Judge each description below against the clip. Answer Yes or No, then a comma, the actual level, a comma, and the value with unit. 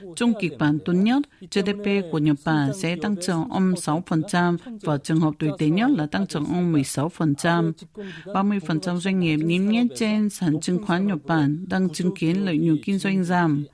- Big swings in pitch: No, average, 3.8 semitones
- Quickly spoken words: No, average, 190 wpm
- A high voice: No, medium, 175 Hz